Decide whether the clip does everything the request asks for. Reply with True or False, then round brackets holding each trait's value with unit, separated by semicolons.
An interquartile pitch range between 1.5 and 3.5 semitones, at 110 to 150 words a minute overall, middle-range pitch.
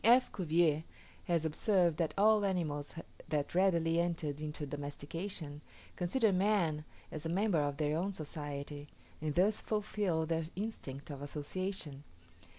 False (4.3 semitones; 135 wpm; 165 Hz)